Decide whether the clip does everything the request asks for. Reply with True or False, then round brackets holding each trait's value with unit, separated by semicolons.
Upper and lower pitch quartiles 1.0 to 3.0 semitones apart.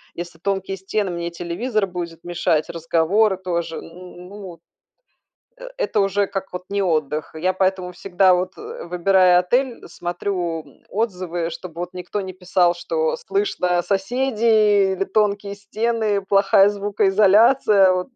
True (2.7 semitones)